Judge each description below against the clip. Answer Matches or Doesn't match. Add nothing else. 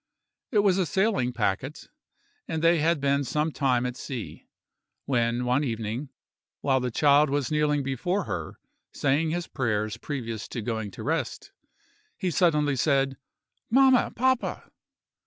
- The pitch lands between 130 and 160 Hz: Matches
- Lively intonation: Doesn't match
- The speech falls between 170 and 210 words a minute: Doesn't match